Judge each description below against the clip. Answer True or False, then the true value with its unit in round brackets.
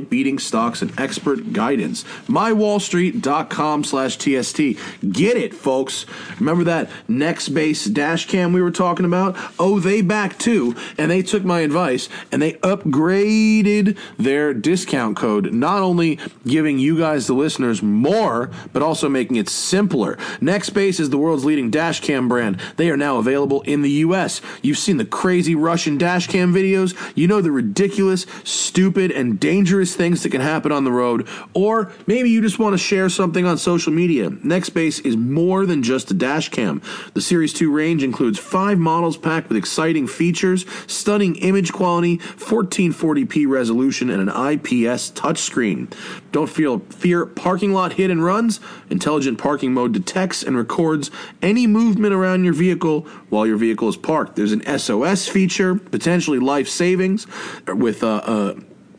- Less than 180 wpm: True (160 wpm)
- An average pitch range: True (4.8 semitones)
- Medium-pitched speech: True (175 Hz)